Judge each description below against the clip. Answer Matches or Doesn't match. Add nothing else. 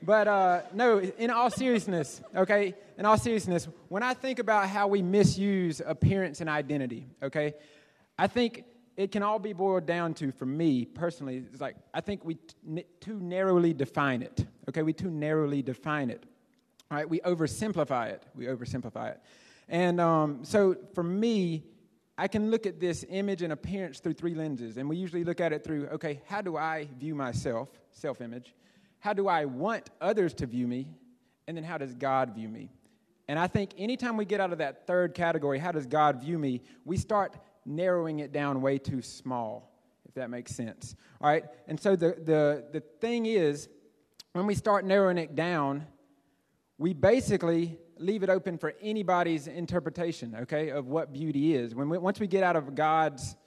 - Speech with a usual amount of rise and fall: Matches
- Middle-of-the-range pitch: Matches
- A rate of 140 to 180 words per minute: Doesn't match